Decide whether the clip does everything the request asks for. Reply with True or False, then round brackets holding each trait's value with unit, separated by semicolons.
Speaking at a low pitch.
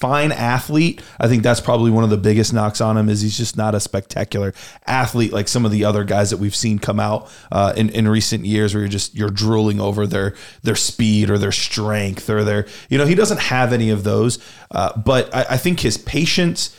True (110 Hz)